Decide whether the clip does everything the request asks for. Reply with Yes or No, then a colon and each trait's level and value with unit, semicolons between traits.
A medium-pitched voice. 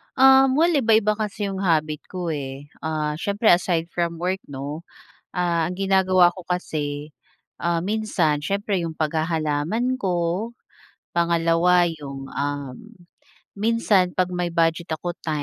Yes: medium, 175 Hz